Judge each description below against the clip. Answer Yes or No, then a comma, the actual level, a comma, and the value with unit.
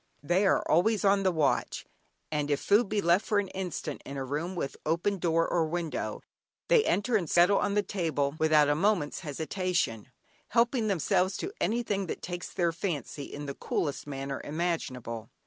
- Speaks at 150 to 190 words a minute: Yes, average, 180 wpm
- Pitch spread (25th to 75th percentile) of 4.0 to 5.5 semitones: Yes, average, 5.2 semitones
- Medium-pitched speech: Yes, medium, 175 Hz